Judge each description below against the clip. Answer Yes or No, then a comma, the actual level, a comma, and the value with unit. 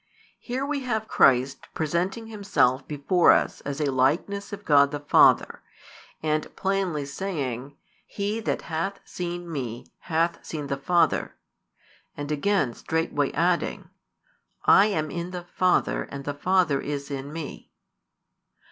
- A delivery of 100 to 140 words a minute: Yes, slow, 135 wpm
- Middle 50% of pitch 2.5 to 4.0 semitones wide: No, average, 5.1 semitones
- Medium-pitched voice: Yes, medium, 160 Hz